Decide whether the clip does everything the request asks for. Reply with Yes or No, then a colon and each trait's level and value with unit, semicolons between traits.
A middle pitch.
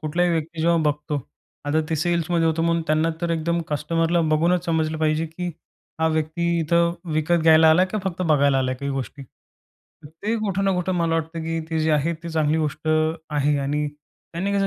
Yes: medium, 160 Hz